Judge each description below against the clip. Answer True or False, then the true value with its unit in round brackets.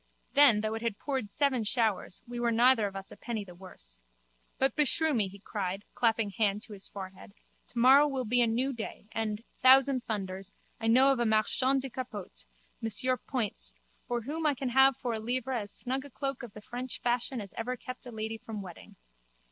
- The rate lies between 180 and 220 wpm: True (205 wpm)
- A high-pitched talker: True (235 Hz)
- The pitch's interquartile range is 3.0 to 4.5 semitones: True (3.7 semitones)